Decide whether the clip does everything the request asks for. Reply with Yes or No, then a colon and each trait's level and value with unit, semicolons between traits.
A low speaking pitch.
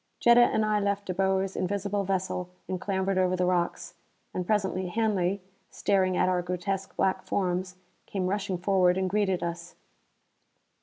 No: high, 190 Hz